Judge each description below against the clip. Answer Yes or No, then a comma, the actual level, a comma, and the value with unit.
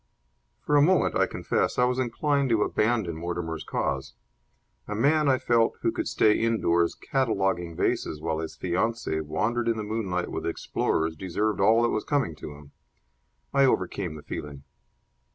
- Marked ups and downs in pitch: Yes, wide, 6.2 semitones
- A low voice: Yes, low, 105 Hz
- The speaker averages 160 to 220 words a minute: Yes, average, 165 wpm